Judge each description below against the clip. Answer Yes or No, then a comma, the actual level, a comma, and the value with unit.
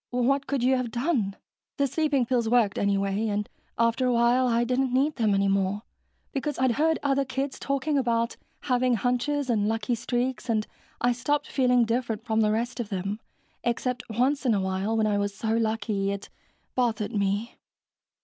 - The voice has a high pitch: Yes, high, 235 Hz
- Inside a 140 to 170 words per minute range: No, average, 180 wpm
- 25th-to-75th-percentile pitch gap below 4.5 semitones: Yes, average, 3.3 semitones